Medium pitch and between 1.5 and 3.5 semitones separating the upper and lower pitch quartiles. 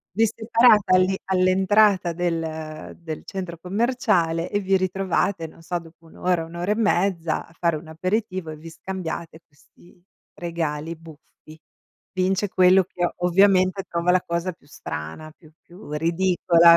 Yes: medium, 175 Hz; narrow, 2.5 semitones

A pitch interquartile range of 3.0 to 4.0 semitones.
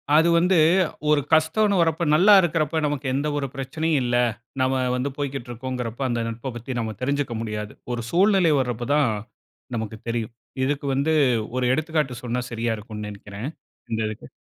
No: average, 4.6 semitones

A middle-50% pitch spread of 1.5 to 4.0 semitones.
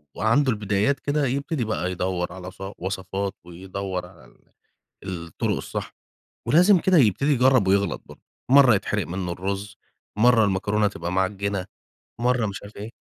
No: average, 4.7 semitones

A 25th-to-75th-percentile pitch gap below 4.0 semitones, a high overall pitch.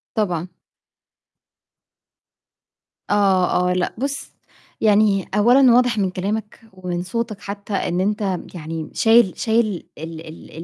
Yes: average, 3.4 semitones; high, 200 Hz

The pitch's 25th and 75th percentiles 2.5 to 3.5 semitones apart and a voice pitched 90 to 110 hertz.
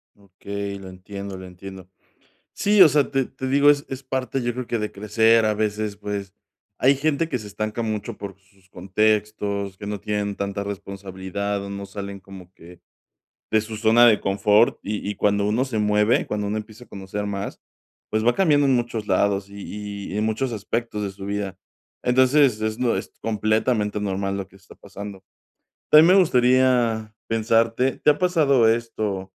Yes: average, 3.1 semitones; low, 105 Hz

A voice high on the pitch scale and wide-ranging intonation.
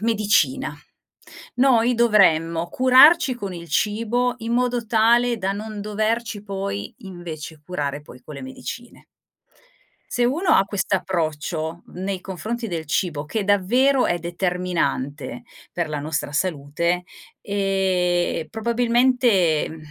Yes: high, 195 Hz; wide, 5.8 semitones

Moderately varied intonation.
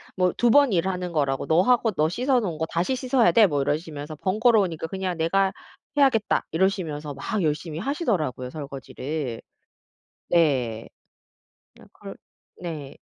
No: wide, 6.1 semitones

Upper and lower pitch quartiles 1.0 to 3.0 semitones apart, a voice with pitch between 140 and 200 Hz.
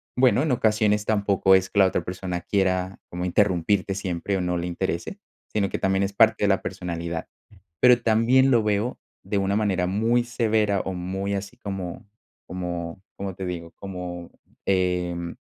No: average, 2.7 semitones; very low, 95 Hz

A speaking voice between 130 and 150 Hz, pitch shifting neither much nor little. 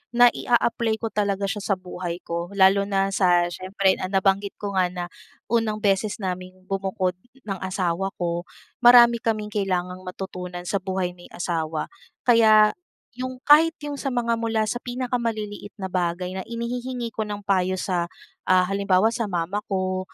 No: high, 195 Hz; average, 3.6 semitones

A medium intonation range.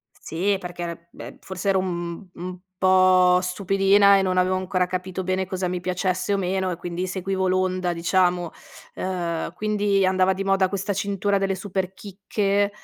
No: narrow, 1.3 semitones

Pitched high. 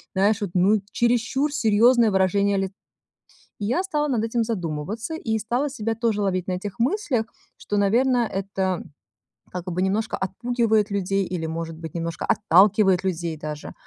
Yes: high, 205 Hz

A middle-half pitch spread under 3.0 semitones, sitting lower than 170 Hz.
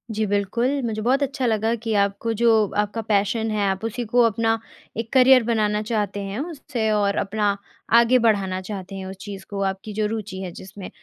No: narrow, 2.5 semitones; high, 215 Hz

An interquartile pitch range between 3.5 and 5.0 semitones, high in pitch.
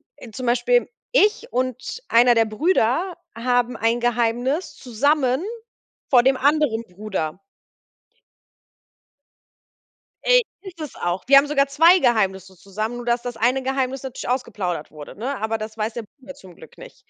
Yes: average, 4.0 semitones; high, 245 Hz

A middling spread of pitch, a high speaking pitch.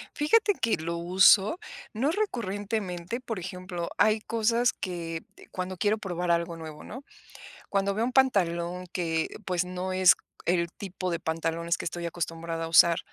No: average, 4.0 semitones; medium, 180 Hz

